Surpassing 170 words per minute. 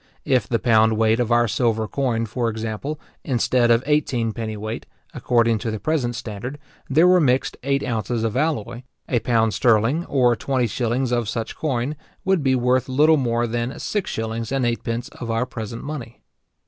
Yes: average, 185 wpm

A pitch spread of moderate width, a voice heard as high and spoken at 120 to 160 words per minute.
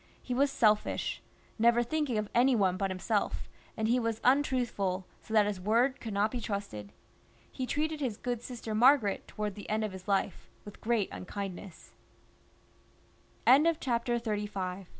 Yes: average, 3.6 semitones; high, 220 Hz; average, 150 wpm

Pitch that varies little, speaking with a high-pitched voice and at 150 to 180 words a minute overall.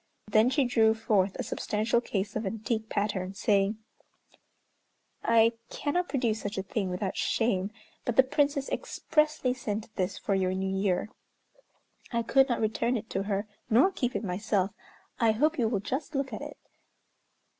No: average, 4.0 semitones; high, 220 Hz; average, 165 wpm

